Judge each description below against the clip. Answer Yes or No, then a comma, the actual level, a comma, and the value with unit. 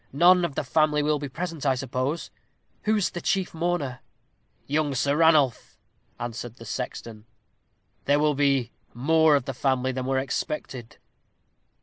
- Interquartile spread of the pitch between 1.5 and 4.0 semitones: Yes, average, 3.6 semitones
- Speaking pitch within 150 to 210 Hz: No, medium, 140 Hz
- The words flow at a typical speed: Yes, average, 150 wpm